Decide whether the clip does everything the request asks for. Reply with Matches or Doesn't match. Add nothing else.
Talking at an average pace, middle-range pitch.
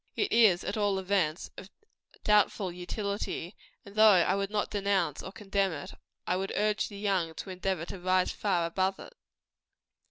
Doesn't match